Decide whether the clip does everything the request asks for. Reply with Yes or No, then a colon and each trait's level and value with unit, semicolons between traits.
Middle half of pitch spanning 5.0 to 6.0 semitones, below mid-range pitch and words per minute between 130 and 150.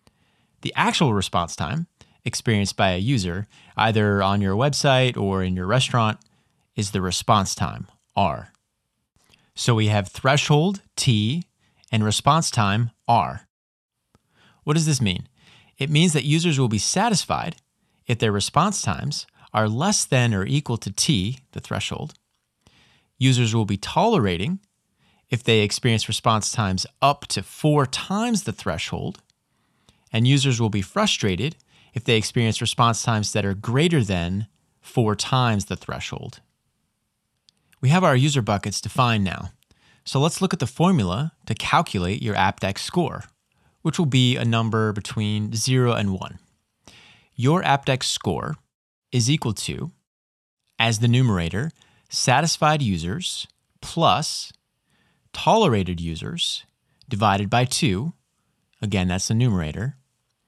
Yes: wide, 5.4 semitones; low, 115 Hz; slow, 135 wpm